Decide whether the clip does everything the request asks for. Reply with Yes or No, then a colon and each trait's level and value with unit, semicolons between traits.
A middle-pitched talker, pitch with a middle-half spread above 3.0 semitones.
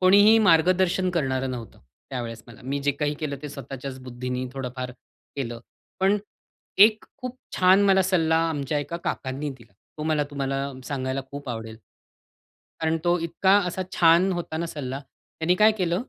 Yes: medium, 150 Hz; wide, 5.4 semitones